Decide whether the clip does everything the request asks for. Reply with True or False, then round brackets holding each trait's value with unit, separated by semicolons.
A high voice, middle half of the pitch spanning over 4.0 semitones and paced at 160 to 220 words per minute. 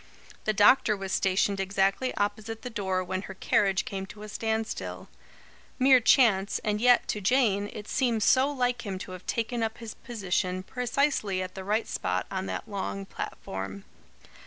False (210 Hz; 3.3 semitones; 170 wpm)